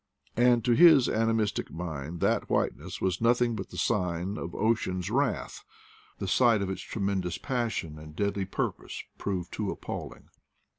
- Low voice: Yes, low, 100 Hz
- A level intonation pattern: No, average, 4.8 semitones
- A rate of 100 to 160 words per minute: Yes, average, 155 wpm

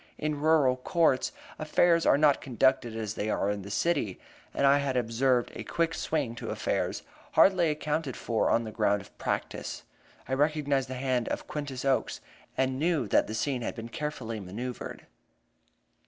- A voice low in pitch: Yes, low, 130 Hz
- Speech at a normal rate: Yes, average, 170 wpm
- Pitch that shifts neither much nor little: Yes, average, 4.6 semitones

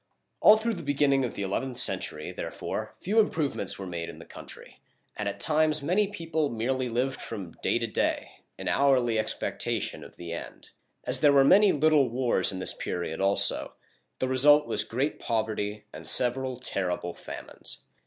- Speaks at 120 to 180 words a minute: Yes, average, 175 wpm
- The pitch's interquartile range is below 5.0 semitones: No, wide, 5.6 semitones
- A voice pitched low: Yes, low, 130 Hz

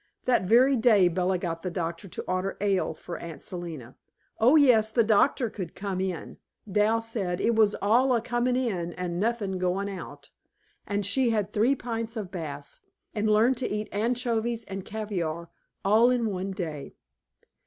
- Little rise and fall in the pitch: No, average, 4.0 semitones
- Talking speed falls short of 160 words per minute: No, average, 170 wpm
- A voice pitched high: Yes, high, 205 Hz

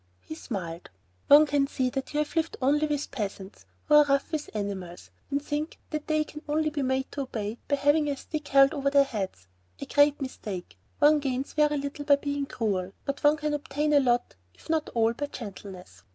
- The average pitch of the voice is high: Yes, very high, 280 Hz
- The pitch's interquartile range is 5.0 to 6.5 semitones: No, average, 4.2 semitones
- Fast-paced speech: Yes, fast, 210 wpm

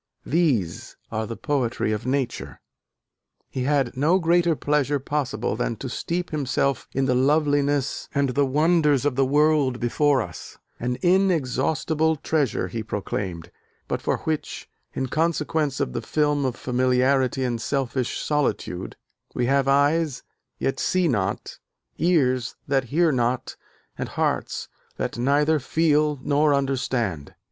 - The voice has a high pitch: No, medium, 140 Hz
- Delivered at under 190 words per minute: Yes, slow, 135 wpm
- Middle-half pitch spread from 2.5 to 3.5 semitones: Yes, average, 3.2 semitones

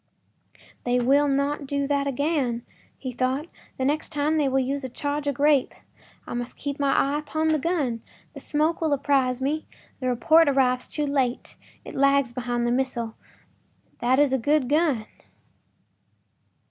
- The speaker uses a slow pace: No, average, 160 wpm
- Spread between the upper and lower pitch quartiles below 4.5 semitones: Yes, narrow, 2.5 semitones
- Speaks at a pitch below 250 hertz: No, very high, 275 Hz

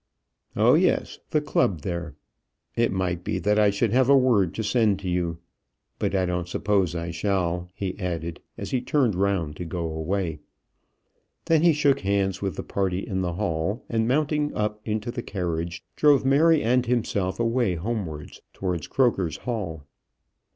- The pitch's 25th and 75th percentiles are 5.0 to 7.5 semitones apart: Yes, average, 5.3 semitones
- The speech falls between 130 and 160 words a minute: No, average, 170 wpm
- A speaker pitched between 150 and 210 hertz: No, low, 100 Hz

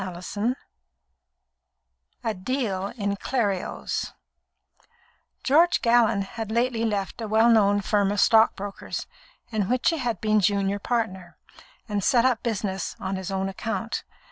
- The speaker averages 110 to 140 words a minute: Yes, slow, 135 wpm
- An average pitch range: Yes, average, 3.0 semitones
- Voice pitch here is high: Yes, high, 215 Hz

